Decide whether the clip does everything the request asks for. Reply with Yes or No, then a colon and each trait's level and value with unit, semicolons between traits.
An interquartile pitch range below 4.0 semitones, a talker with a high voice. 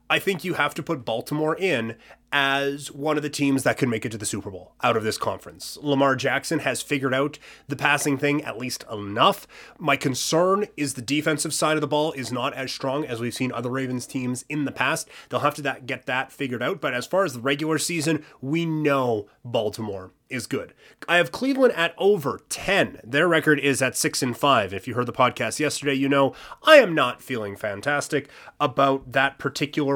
No: average, 3.0 semitones; medium, 140 Hz